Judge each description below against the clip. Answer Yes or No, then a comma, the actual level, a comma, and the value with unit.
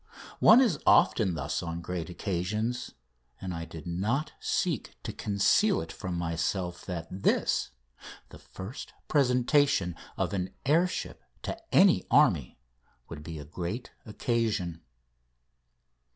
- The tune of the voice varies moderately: No, wide, 6.4 semitones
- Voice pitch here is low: Yes, very low, 95 Hz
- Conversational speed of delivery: No, slow, 125 wpm